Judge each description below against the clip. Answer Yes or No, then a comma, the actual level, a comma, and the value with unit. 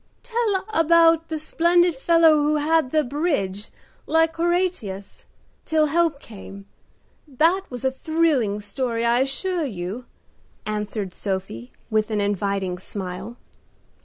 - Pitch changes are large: Yes, wide, 8.1 semitones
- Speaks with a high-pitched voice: Yes, very high, 270 Hz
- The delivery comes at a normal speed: No, slow, 125 wpm